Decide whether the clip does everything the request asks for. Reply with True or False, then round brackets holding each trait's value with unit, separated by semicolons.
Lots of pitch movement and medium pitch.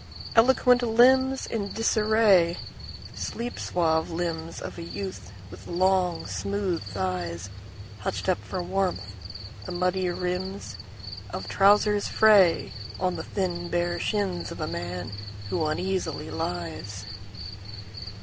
True (8.3 semitones; 180 Hz)